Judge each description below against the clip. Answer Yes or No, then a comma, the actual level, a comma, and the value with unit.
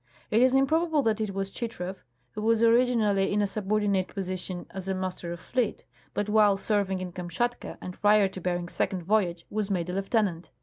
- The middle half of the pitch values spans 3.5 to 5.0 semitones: No, average, 2.9 semitones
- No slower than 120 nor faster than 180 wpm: No, average, 190 wpm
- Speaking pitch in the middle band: No, high, 200 Hz